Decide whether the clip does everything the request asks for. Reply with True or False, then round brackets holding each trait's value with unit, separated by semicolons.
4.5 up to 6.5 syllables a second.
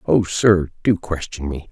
False (4.1 syllables/s)